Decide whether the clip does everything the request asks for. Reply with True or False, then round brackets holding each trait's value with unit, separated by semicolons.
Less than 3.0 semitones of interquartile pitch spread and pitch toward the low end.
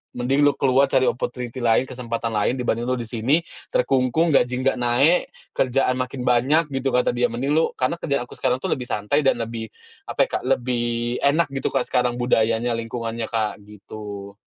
True (2.5 semitones; 125 Hz)